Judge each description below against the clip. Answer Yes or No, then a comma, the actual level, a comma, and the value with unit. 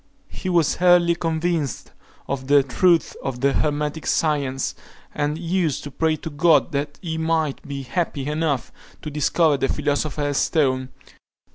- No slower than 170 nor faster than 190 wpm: No, average, 145 wpm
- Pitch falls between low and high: Yes, medium, 150 Hz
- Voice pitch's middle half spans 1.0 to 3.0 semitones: Yes, average, 2.7 semitones